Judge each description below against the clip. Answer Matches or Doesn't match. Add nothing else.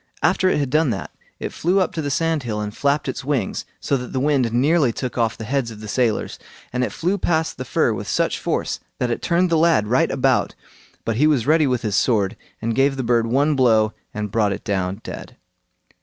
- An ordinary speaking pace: Doesn't match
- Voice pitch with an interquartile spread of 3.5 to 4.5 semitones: Doesn't match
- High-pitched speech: Doesn't match